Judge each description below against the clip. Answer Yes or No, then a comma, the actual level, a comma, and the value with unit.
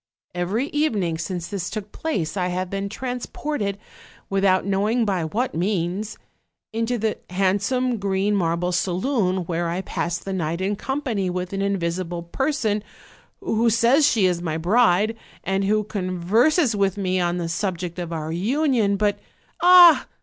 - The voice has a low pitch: No, high, 195 Hz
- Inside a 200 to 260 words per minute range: No, average, 155 wpm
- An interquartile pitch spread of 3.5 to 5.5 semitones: Yes, average, 4.0 semitones